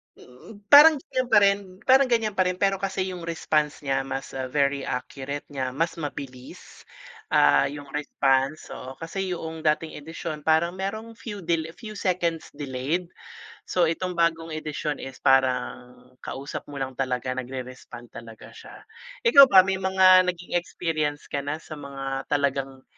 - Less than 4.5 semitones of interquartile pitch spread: No, average, 5.3 semitones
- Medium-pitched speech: Yes, medium, 155 Hz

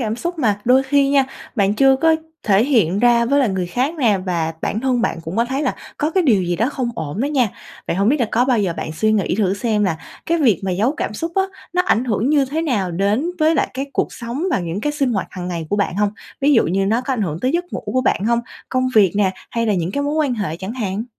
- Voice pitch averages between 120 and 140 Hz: No, high, 230 Hz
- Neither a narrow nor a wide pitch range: No, wide, 5.7 semitones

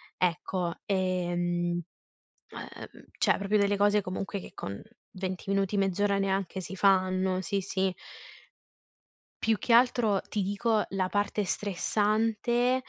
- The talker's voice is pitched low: No, high, 195 Hz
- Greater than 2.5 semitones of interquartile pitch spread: No, narrow, 2.0 semitones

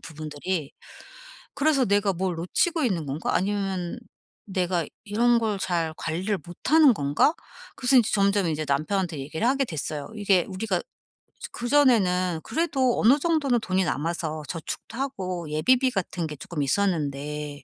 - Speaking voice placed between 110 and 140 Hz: No, medium, 185 Hz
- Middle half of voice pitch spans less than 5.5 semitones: No, wide, 6.8 semitones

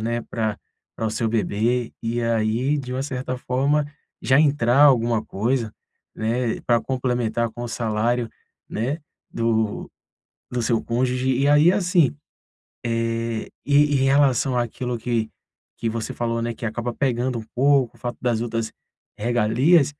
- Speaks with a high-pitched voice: No, low, 120 Hz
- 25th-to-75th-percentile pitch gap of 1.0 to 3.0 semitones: Yes, narrow, 2.4 semitones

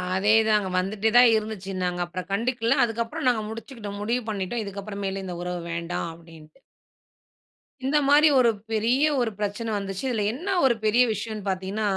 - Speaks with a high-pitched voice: Yes, high, 215 Hz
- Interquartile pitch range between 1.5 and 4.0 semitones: Yes, average, 3.3 semitones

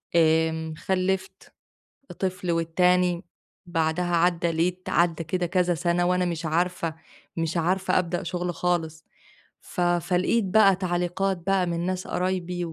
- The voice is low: No, medium, 175 Hz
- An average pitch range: No, narrow, 1.4 semitones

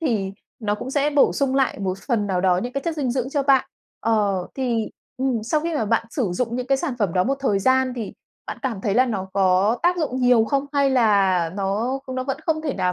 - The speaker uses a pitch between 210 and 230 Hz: No, high, 245 Hz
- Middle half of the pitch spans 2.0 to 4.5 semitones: No, average, 5.1 semitones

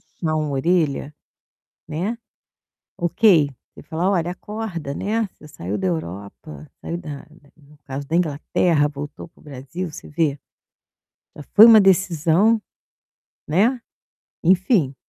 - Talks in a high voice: No, medium, 160 Hz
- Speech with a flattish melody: No, average, 4.3 semitones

